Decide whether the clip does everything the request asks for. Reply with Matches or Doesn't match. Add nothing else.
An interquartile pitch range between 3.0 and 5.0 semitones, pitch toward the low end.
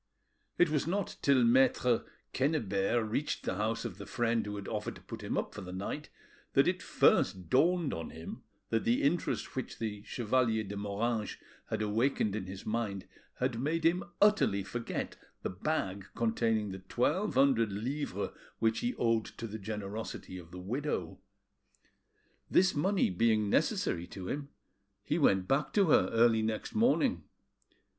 Doesn't match